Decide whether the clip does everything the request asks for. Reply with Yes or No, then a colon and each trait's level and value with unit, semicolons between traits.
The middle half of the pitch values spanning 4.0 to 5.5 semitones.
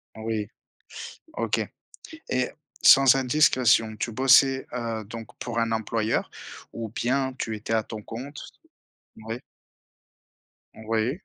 No: average, 2.9 semitones